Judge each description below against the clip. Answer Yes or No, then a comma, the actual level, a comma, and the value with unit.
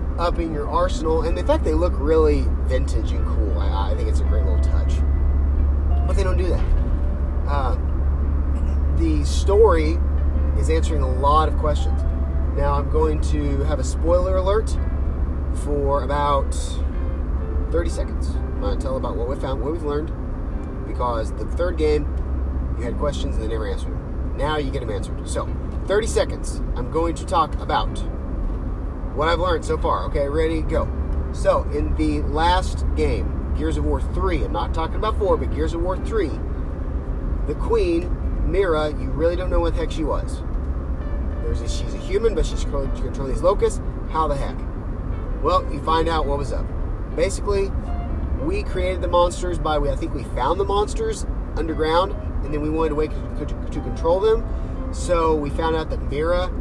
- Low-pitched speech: Yes, very low, 70 Hz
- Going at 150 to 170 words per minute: No, average, 180 wpm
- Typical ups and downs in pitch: No, narrow, 2.3 semitones